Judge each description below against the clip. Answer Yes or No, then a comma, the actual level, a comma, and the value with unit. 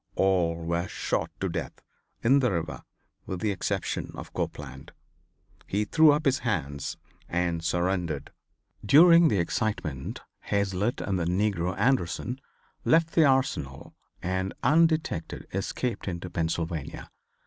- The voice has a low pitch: Yes, very low, 95 Hz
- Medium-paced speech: No, slow, 125 wpm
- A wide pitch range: Yes, wide, 7.1 semitones